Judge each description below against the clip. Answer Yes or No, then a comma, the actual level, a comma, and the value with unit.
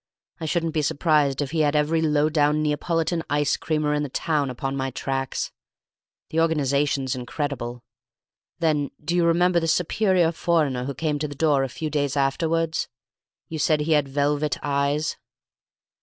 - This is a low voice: No, medium, 150 Hz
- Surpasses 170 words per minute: No, average, 165 wpm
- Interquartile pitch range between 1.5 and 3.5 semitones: Yes, narrow, 2.5 semitones